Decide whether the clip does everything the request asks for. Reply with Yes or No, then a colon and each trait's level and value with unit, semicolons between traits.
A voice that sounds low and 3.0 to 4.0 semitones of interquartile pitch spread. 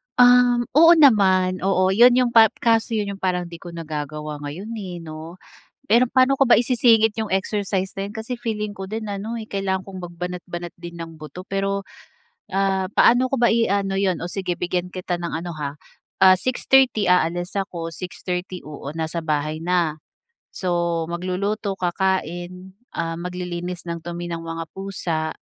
No: medium, 185 Hz; average, 3.6 semitones